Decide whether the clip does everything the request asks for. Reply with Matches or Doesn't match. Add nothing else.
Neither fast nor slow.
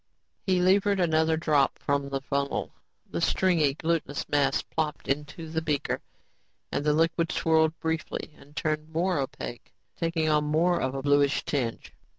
Matches